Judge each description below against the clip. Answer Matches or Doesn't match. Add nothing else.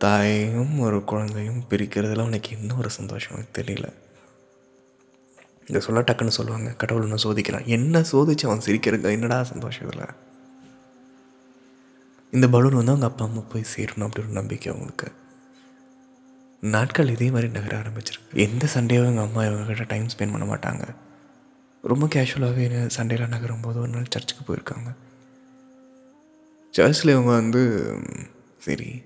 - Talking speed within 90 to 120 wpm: Doesn't match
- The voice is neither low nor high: Doesn't match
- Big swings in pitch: Doesn't match